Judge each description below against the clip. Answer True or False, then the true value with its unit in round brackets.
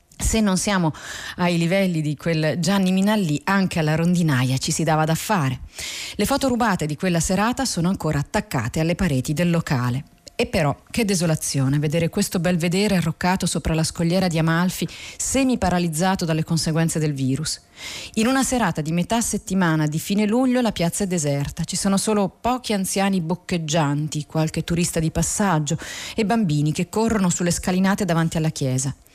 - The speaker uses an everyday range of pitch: True (3.8 semitones)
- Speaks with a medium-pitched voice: True (175 Hz)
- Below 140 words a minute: False (165 wpm)